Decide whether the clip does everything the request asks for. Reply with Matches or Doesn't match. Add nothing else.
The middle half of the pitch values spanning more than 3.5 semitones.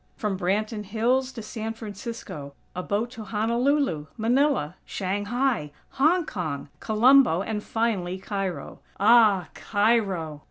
Matches